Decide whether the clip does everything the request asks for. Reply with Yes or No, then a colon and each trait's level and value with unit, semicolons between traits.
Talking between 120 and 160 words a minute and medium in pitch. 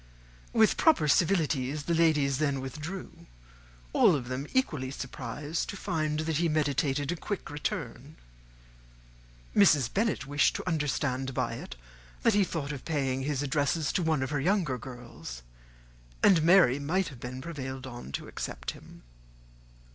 Yes: average, 150 wpm; medium, 145 Hz